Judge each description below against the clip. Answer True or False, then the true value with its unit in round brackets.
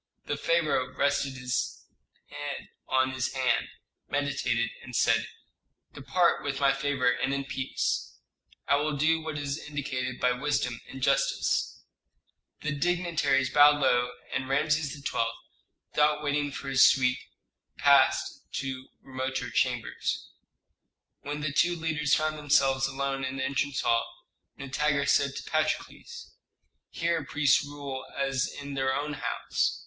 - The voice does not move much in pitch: True (1.9 semitones)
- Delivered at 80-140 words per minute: True (135 wpm)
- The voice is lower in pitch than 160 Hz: True (140 Hz)